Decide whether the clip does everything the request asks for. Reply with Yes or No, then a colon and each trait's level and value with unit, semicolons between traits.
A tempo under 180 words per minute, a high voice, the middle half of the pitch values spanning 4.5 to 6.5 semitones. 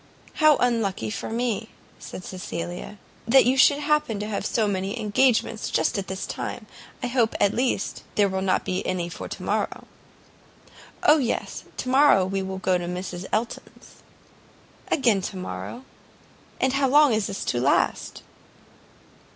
Yes: average, 155 wpm; high, 210 Hz; average, 5.1 semitones